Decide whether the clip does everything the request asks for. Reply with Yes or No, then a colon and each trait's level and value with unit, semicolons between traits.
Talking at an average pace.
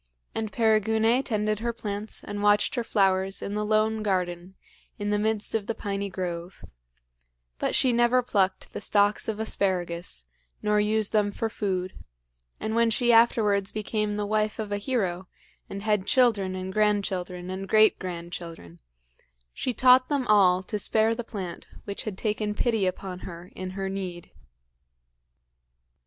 Yes: average, 155 wpm